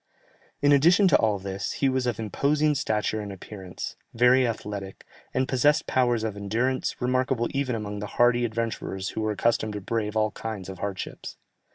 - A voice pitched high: No, low, 115 Hz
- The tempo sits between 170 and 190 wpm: Yes, average, 175 wpm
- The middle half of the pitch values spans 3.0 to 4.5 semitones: Yes, average, 3.8 semitones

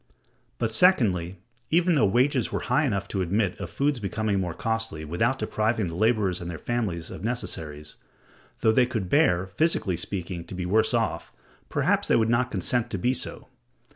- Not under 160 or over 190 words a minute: Yes, average, 180 wpm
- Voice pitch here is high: No, low, 110 Hz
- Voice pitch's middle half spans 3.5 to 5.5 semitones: Yes, average, 5.1 semitones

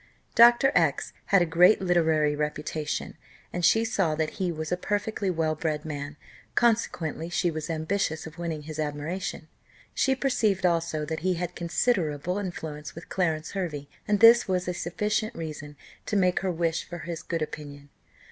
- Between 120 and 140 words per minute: No, average, 165 wpm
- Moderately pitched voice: Yes, medium, 170 Hz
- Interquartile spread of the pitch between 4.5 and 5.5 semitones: No, average, 3.5 semitones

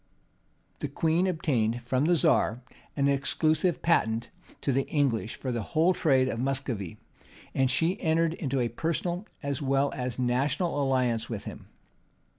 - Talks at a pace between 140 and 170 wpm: Yes, average, 150 wpm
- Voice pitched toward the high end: No, low, 135 Hz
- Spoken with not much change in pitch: No, average, 4.6 semitones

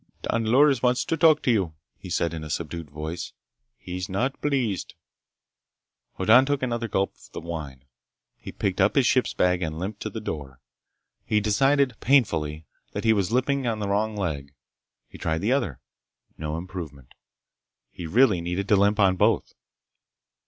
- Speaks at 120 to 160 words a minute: No, average, 170 wpm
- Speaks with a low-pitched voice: Yes, low, 100 Hz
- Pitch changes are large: Yes, wide, 6.7 semitones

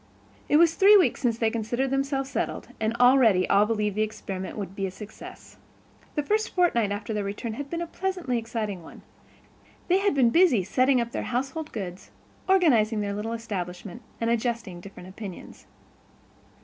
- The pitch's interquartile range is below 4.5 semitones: No, average, 4.9 semitones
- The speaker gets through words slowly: No, average, 175 wpm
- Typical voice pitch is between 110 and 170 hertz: No, high, 230 Hz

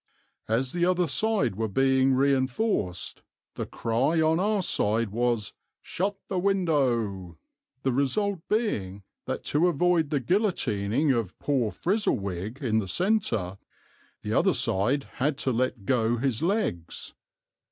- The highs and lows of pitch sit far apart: Yes, wide, 7.9 semitones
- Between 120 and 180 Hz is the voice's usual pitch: Yes, low, 135 Hz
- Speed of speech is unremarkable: No, slow, 130 wpm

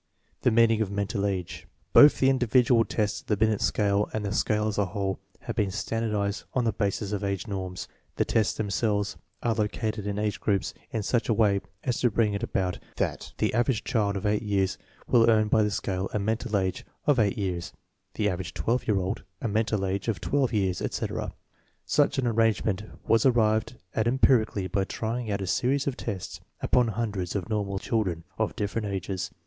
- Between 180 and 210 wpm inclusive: Yes, average, 200 wpm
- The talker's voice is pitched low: Yes, low, 105 Hz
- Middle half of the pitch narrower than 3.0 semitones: Yes, narrow, 2.4 semitones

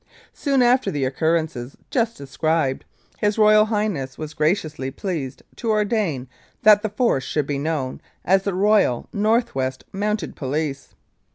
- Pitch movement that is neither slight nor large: No, wide, 7.5 semitones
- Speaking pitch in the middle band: Yes, medium, 165 Hz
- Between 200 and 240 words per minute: No, average, 145 wpm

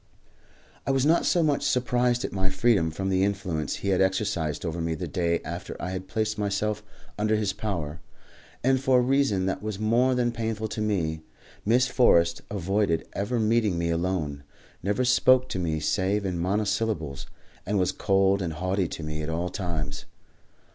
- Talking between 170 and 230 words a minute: Yes, average, 180 wpm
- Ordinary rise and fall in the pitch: Yes, average, 4.6 semitones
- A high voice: No, low, 100 Hz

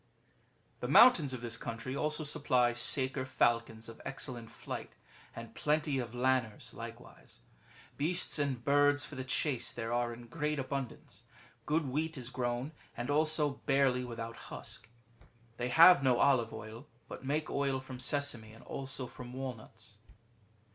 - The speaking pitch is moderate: No, low, 130 Hz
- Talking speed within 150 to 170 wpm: Yes, average, 155 wpm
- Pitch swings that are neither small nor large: Yes, average, 3.2 semitones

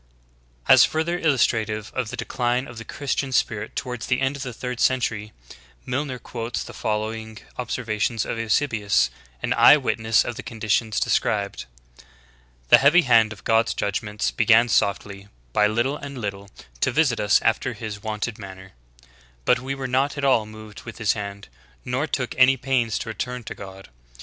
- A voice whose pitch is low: Yes, low, 115 Hz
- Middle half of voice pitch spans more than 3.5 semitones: No, average, 3.1 semitones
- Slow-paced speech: No, average, 180 wpm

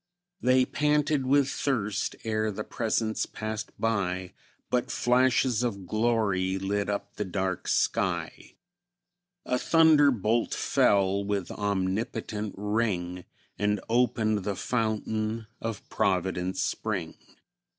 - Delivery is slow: Yes, slow, 105 wpm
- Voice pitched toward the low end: Yes, low, 110 Hz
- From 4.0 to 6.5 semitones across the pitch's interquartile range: No, average, 3.3 semitones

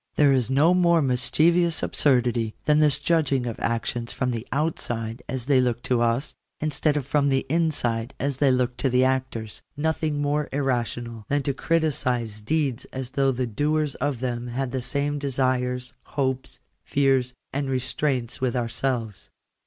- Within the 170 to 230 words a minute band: No, average, 160 wpm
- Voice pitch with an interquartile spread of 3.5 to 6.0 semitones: No, average, 3.0 semitones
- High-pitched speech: No, low, 130 Hz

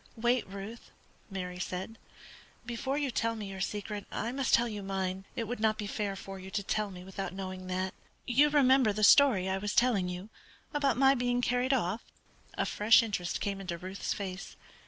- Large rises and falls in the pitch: No, average, 4.0 semitones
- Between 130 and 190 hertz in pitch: No, high, 210 Hz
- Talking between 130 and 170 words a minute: No, average, 195 wpm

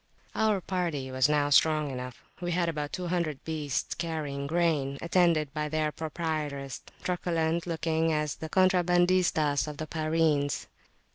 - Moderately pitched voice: Yes, medium, 160 Hz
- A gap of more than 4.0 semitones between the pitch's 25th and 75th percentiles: No, average, 2.7 semitones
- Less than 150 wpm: Yes, slow, 135 wpm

